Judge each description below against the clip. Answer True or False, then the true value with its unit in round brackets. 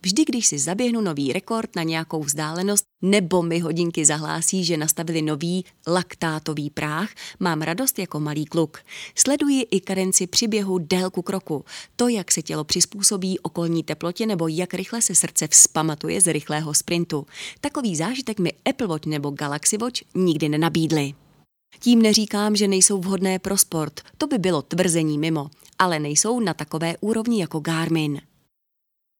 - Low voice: False (175 Hz)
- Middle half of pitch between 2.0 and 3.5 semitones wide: False (4.4 semitones)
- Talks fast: False (150 wpm)